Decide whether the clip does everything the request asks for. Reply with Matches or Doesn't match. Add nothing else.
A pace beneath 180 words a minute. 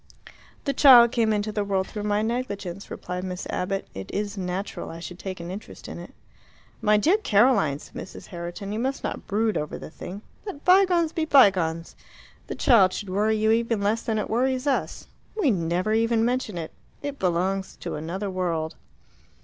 Doesn't match